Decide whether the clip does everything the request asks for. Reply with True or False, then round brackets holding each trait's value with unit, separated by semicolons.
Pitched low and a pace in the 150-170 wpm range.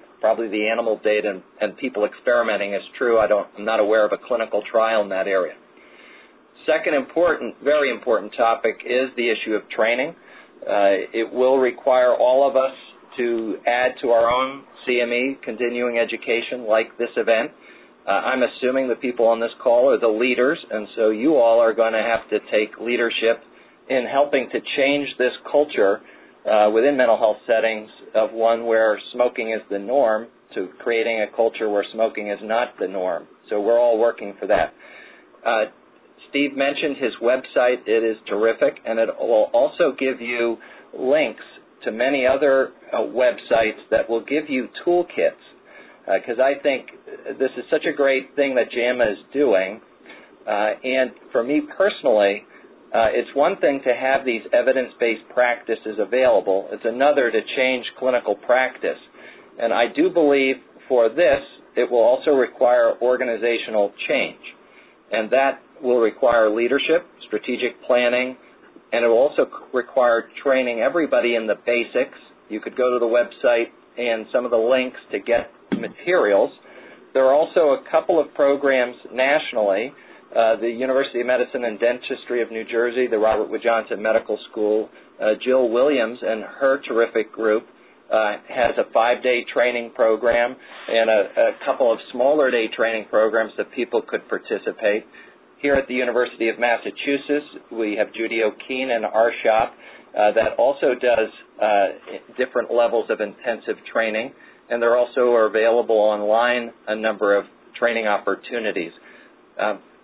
True (120 Hz; 160 wpm)